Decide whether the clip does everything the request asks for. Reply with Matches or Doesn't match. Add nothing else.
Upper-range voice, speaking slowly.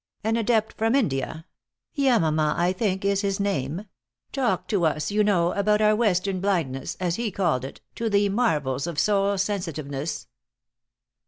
Doesn't match